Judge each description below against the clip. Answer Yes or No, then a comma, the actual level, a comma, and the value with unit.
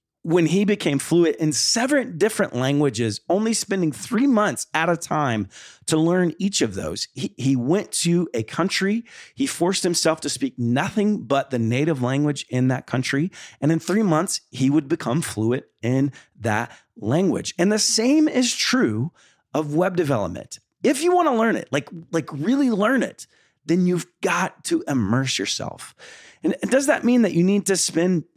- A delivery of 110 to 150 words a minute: No, average, 180 wpm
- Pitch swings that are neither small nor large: No, wide, 6.8 semitones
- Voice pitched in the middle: Yes, medium, 170 Hz